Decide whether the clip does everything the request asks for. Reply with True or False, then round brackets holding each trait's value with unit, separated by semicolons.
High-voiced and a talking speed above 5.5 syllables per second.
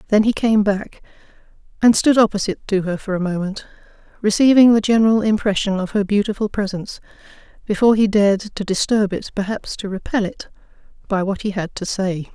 True (205 Hz; 5.9 syllables/s)